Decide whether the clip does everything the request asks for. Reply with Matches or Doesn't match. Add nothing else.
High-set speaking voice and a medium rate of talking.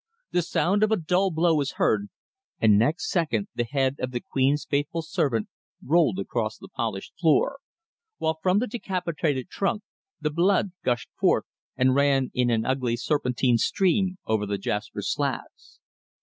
Doesn't match